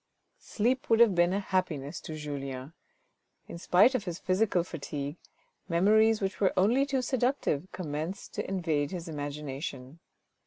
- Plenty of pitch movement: Yes, wide, 5.9 semitones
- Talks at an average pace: Yes, average, 145 wpm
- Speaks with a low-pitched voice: No, medium, 180 Hz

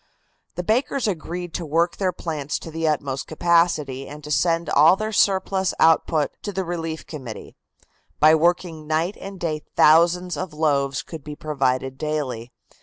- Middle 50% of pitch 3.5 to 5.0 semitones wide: No, average, 3.0 semitones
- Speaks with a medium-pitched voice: Yes, medium, 160 Hz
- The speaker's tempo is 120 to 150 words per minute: No, average, 160 wpm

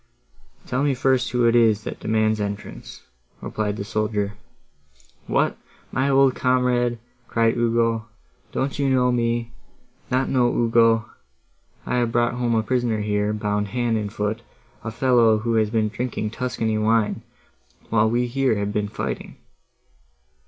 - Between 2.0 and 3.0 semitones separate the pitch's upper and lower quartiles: Yes, narrow, 2.4 semitones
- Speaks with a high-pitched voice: No, low, 115 Hz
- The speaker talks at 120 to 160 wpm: Yes, average, 145 wpm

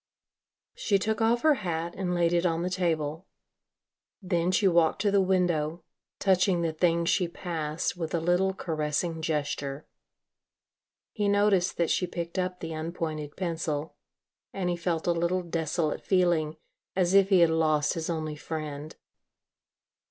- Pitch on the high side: No, medium, 170 Hz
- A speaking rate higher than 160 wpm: No, average, 150 wpm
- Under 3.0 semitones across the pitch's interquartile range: Yes, narrow, 2.5 semitones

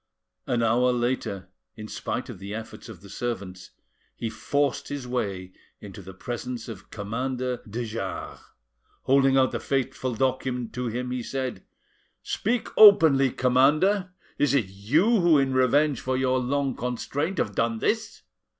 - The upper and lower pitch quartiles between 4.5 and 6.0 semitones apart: No, average, 3.4 semitones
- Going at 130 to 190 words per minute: Yes, average, 150 wpm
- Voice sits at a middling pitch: No, low, 125 Hz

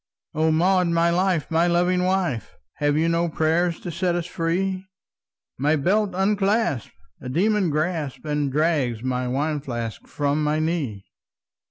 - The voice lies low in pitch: No, medium, 165 Hz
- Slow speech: No, average, 150 wpm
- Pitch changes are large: No, average, 3.7 semitones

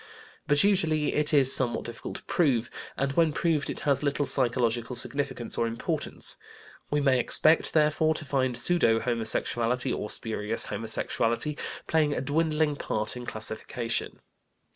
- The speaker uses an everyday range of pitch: Yes, average, 4.3 semitones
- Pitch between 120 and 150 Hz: Yes, low, 135 Hz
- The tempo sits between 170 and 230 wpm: No, average, 140 wpm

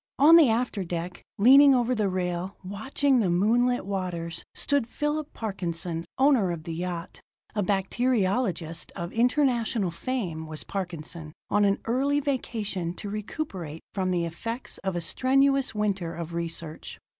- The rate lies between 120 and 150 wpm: Yes, average, 145 wpm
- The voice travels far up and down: Yes, wide, 6.4 semitones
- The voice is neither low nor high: No, high, 200 Hz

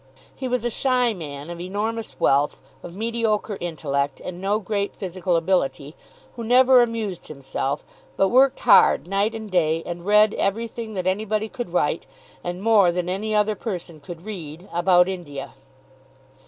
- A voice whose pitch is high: Yes, high, 195 Hz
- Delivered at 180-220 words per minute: No, average, 155 wpm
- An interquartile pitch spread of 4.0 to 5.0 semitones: Yes, average, 4.3 semitones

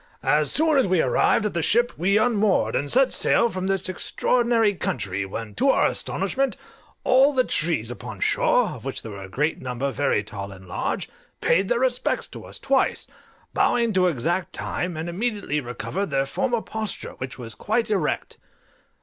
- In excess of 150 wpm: Yes, average, 180 wpm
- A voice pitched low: No, medium, 185 Hz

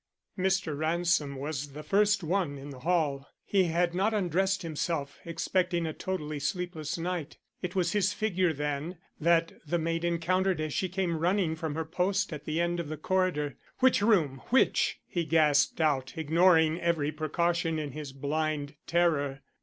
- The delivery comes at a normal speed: Yes, average, 165 wpm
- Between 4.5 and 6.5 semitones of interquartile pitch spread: No, average, 3.2 semitones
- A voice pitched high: No, medium, 165 Hz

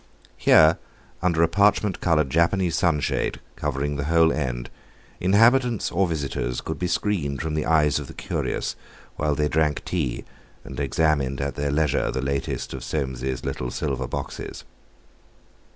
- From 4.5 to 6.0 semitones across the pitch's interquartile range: No, average, 3.5 semitones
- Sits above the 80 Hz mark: No, very low, 75 Hz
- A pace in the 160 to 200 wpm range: No, average, 150 wpm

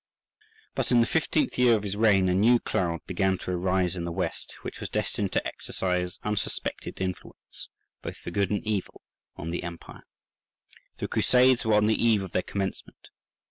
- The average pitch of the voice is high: No, low, 100 Hz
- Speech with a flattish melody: No, average, 3.3 semitones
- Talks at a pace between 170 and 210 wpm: Yes, average, 180 wpm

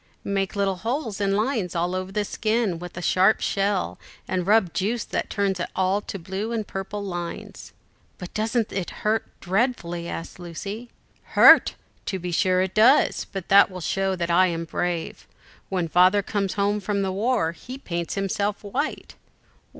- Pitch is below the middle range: No, high, 195 Hz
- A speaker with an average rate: Yes, average, 175 wpm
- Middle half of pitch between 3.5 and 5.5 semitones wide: No, average, 2.8 semitones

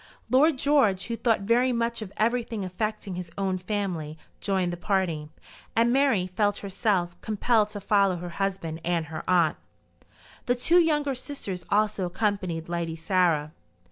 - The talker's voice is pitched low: No, high, 195 Hz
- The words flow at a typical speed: Yes, average, 150 wpm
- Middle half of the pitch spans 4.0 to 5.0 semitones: Yes, average, 4.6 semitones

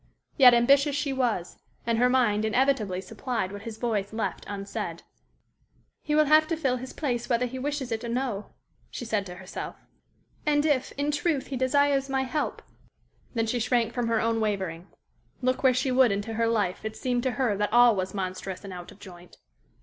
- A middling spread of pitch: Yes, average, 4.2 semitones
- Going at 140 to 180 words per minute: No, average, 200 wpm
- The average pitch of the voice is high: Yes, high, 240 Hz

